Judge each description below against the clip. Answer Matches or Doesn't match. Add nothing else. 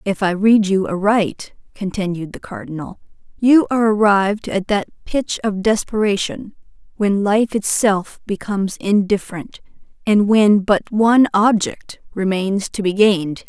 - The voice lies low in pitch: Doesn't match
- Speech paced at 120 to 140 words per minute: Matches